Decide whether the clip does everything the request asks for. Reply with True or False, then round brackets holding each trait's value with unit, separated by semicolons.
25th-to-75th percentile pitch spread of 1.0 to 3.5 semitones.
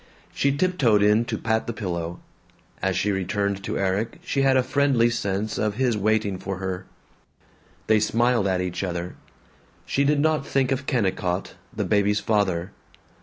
False (4.6 semitones)